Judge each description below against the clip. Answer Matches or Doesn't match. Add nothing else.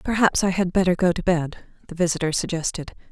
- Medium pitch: Matches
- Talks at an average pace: Matches